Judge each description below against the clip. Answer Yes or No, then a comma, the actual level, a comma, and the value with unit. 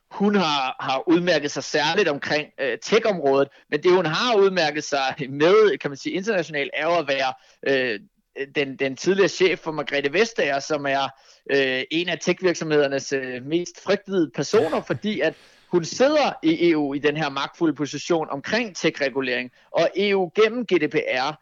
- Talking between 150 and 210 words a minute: Yes, average, 160 wpm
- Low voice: No, medium, 155 Hz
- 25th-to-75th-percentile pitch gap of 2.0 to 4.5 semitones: No, average, 5.0 semitones